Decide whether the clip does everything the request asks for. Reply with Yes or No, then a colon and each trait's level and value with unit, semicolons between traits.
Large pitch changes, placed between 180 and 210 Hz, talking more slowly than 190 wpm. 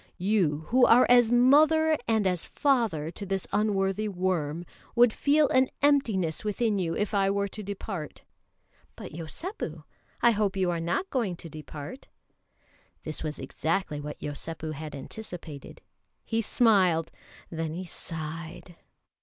Yes: wide, 5.7 semitones; high, 190 Hz; average, 140 wpm